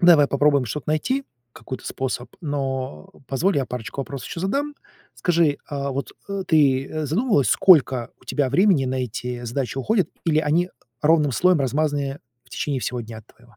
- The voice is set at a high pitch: No, medium, 145 Hz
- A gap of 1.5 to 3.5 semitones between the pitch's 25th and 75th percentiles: No, average, 4.1 semitones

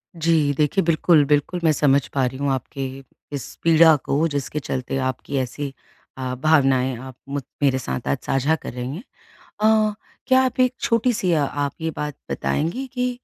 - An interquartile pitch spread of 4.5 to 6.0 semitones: No, average, 3.6 semitones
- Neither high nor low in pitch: Yes, medium, 145 Hz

